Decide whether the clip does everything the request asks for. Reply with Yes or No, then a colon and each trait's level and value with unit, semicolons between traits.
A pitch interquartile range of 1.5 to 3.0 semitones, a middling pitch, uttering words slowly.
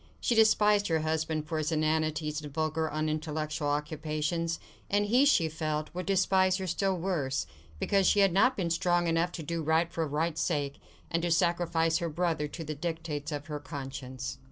No: narrow, 2.4 semitones; medium, 160 Hz; average, 180 wpm